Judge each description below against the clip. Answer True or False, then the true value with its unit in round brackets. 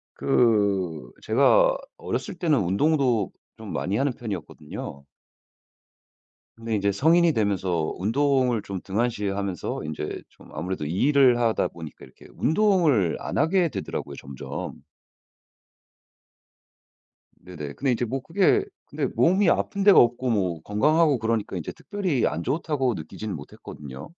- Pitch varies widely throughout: True (7.7 semitones)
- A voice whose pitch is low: True (115 Hz)